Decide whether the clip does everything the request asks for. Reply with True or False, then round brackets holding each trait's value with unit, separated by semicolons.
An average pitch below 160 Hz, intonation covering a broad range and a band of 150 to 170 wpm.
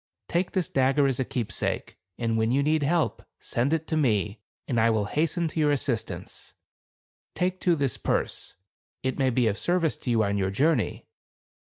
False (135 Hz; 5.7 semitones; 205 wpm)